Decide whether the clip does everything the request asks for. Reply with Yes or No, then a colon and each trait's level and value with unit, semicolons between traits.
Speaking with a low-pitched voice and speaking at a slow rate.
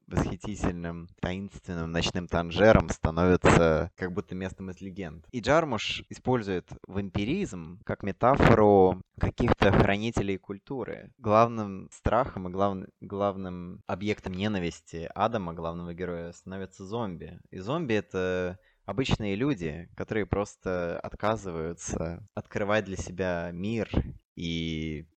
Yes: very low, 95 Hz; slow, 105 wpm